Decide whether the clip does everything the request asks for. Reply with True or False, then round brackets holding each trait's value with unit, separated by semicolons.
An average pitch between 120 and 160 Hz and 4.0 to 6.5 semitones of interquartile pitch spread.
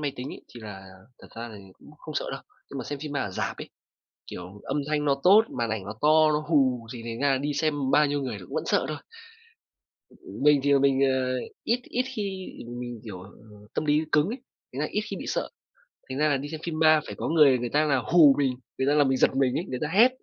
False (140 Hz; 3.3 semitones)